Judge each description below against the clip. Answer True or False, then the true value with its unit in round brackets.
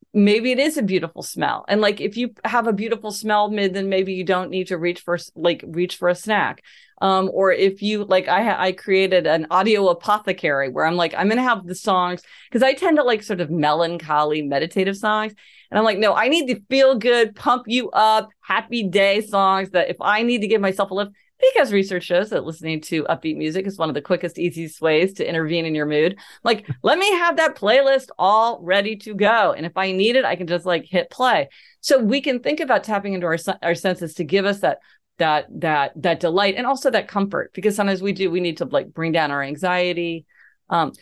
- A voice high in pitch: True (195 Hz)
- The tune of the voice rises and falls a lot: False (3.9 semitones)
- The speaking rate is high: True (230 wpm)